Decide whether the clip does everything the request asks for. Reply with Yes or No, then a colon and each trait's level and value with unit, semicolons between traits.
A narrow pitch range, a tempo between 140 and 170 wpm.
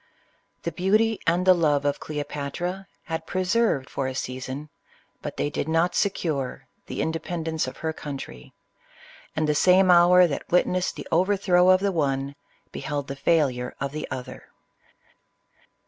No: average, 4.3 semitones; average, 145 wpm